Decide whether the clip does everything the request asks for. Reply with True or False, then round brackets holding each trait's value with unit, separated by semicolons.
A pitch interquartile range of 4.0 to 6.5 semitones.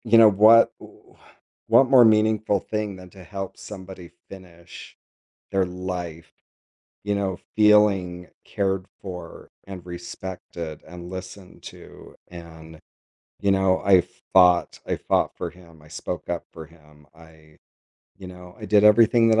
False (2.8 semitones)